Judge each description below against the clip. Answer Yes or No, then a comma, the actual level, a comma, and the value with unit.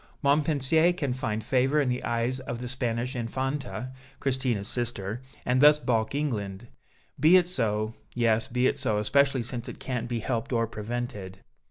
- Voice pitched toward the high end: No, low, 125 Hz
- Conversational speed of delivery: Yes, average, 165 wpm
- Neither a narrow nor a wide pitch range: Yes, average, 3.0 semitones